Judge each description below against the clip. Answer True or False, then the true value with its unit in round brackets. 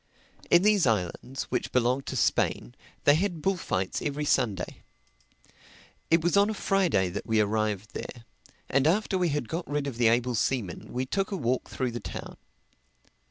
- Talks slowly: False (170 wpm)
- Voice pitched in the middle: False (130 Hz)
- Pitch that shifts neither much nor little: False (7.2 semitones)